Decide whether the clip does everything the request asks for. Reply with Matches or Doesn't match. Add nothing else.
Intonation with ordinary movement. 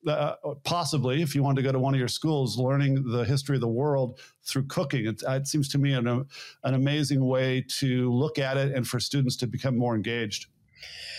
Doesn't match